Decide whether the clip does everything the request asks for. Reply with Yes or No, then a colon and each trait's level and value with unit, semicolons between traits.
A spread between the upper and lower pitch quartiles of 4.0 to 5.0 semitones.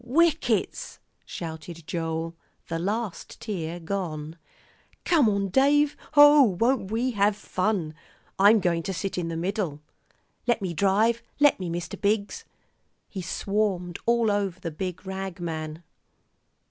Yes: average, 4.6 semitones